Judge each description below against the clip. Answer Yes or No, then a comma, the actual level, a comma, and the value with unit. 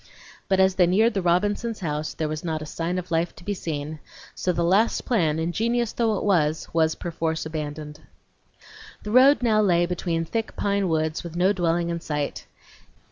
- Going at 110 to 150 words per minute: No, average, 190 wpm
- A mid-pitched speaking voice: Yes, medium, 175 Hz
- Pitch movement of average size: Yes, average, 4.1 semitones